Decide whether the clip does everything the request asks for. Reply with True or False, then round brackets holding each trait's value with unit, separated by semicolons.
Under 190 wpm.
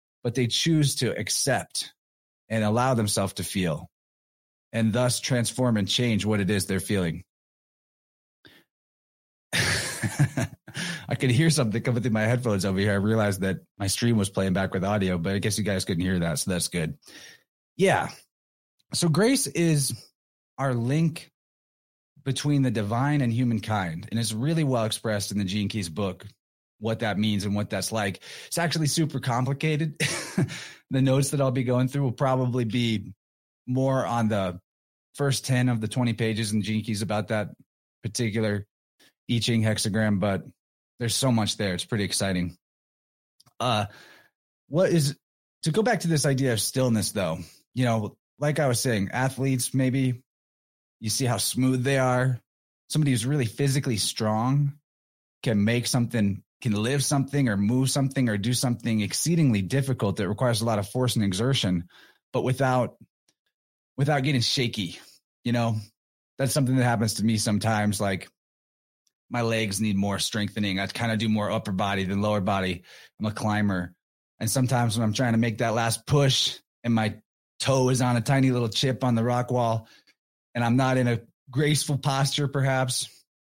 True (170 wpm)